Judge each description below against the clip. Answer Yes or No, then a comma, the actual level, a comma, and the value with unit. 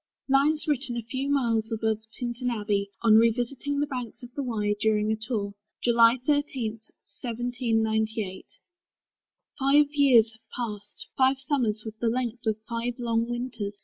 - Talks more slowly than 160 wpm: Yes, average, 145 wpm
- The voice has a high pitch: Yes, high, 235 Hz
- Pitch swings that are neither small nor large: Yes, average, 3.0 semitones